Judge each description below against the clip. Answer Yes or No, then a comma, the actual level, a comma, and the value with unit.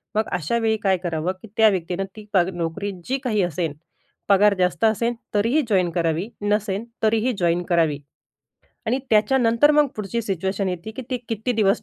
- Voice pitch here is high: Yes, high, 205 Hz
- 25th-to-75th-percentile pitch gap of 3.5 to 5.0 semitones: Yes, average, 4.0 semitones